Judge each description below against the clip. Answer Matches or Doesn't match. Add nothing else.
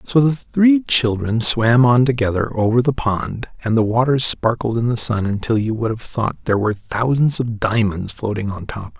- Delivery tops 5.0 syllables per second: Doesn't match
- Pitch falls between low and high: Doesn't match